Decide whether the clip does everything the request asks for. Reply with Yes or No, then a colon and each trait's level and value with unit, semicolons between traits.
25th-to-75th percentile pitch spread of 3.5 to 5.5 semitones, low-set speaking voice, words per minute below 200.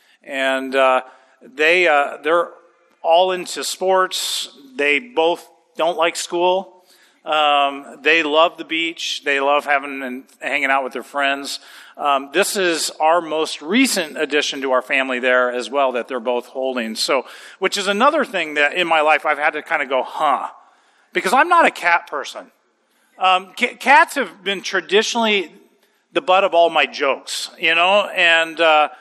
No: average, 4.7 semitones; medium, 160 Hz; average, 170 wpm